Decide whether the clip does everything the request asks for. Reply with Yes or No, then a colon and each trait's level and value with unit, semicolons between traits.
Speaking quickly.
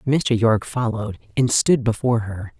No: average, 160 wpm